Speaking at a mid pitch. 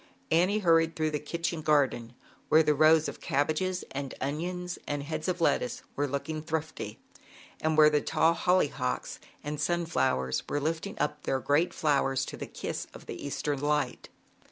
Yes: medium, 155 Hz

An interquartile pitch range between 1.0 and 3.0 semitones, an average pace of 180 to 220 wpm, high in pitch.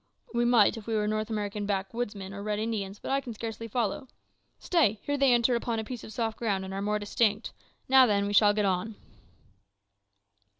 Yes: narrow, 2.5 semitones; fast, 205 wpm; high, 215 Hz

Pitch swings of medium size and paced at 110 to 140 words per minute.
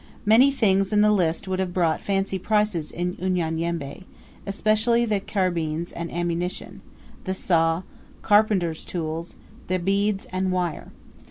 Yes: average, 3.2 semitones; slow, 135 wpm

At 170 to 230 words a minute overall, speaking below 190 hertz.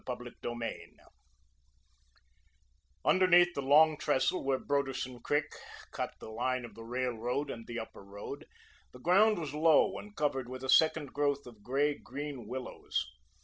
No: average, 145 wpm; low, 135 Hz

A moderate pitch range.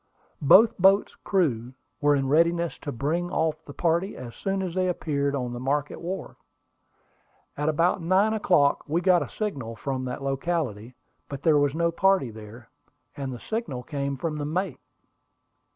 Yes: average, 4.6 semitones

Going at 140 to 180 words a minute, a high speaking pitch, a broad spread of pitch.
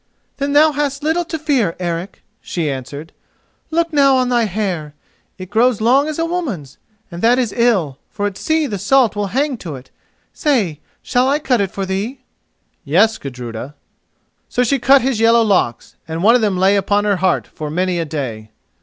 No: average, 190 wpm; high, 210 Hz; wide, 7.6 semitones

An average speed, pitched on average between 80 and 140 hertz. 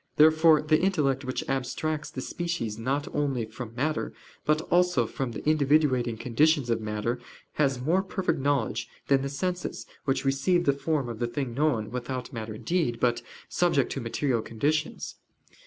Yes: average, 160 wpm; low, 135 Hz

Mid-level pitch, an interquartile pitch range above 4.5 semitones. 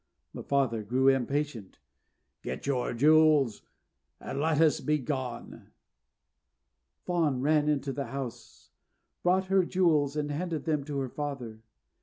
No: medium, 145 Hz; average, 3.0 semitones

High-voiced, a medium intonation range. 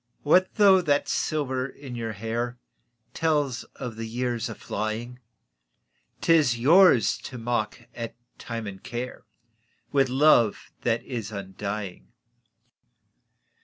No: low, 120 Hz; average, 3.9 semitones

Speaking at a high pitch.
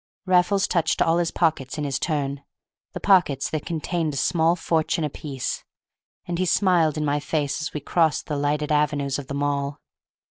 No: medium, 150 Hz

